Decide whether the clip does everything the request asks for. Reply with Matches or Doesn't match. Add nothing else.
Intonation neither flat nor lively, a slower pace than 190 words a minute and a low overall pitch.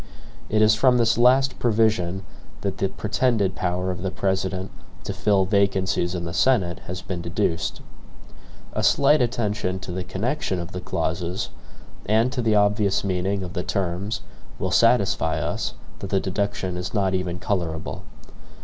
Matches